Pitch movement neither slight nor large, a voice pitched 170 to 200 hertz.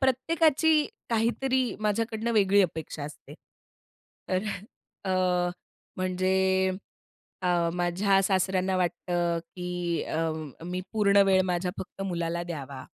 Yes: average, 3.5 semitones; high, 190 Hz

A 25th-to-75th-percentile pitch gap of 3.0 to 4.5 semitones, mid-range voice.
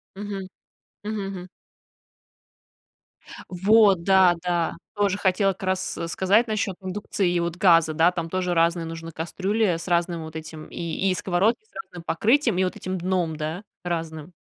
No: narrow, 2.6 semitones; medium, 180 Hz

